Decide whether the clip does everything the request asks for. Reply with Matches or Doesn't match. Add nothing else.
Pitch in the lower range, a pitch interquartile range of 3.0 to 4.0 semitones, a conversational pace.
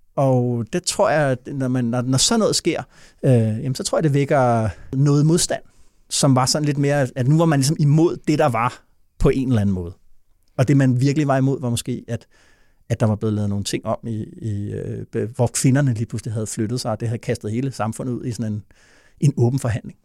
Doesn't match